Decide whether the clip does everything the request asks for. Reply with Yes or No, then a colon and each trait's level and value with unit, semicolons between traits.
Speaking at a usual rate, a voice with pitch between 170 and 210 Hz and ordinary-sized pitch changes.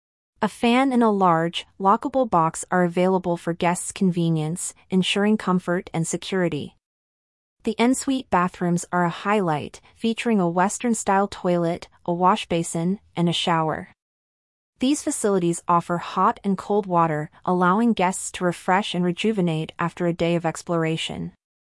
Yes: average, 145 wpm; medium, 180 Hz; average, 3.2 semitones